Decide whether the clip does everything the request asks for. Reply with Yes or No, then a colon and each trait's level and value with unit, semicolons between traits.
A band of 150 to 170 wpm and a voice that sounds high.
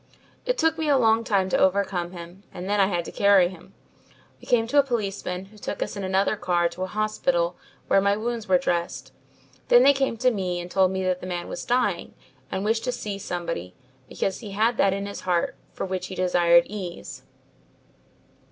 No: fast, 205 wpm; high, 195 Hz